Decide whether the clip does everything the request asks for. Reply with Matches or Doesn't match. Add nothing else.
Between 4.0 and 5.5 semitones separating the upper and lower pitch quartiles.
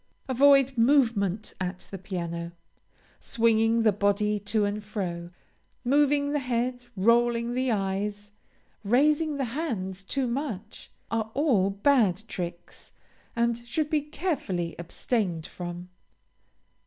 Matches